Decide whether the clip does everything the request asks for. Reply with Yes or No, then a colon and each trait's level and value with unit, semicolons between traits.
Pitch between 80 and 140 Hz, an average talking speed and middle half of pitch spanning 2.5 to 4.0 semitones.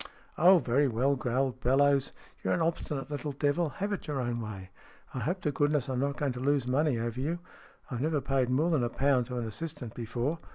No: low, 135 Hz; fast, 215 wpm; average, 3.2 semitones